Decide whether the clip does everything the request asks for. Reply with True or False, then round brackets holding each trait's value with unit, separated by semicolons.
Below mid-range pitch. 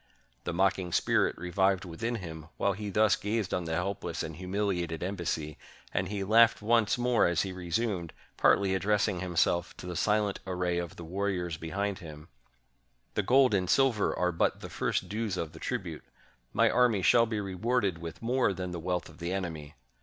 True (95 Hz)